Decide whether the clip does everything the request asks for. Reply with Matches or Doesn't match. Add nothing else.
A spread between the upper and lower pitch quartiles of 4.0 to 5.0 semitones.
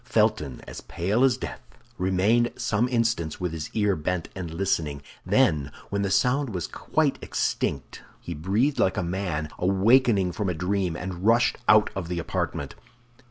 Matches